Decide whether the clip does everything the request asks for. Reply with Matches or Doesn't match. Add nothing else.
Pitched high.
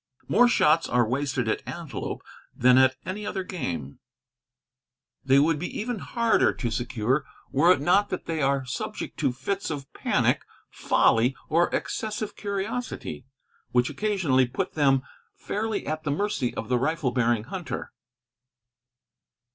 Doesn't match